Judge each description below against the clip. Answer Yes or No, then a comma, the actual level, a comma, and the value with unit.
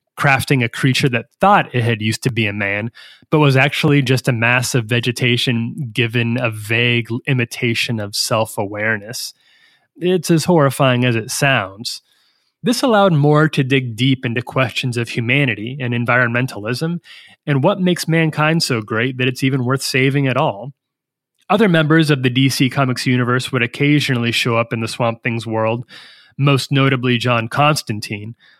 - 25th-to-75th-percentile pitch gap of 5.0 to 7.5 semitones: No, average, 3.2 semitones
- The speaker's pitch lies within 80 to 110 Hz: No, low, 130 Hz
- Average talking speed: Yes, average, 165 wpm